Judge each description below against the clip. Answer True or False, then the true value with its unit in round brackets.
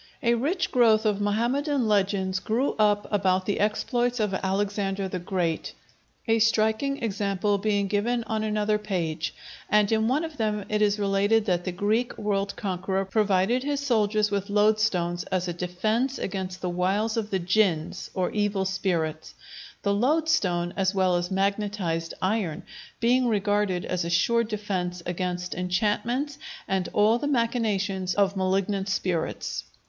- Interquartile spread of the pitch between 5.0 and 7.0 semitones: False (2.7 semitones)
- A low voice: False (205 Hz)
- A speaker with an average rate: True (150 wpm)